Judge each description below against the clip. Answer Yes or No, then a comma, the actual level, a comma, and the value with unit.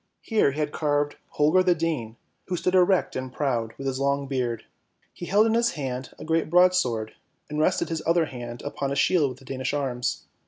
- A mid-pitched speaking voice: Yes, medium, 145 Hz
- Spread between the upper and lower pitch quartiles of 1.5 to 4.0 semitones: No, average, 4.8 semitones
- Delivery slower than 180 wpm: No, fast, 205 wpm